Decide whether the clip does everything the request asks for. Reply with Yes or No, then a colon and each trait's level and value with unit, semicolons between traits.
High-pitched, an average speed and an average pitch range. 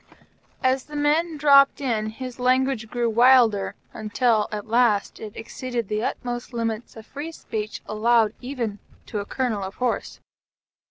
Yes: high, 235 Hz; average, 150 wpm; average, 3.2 semitones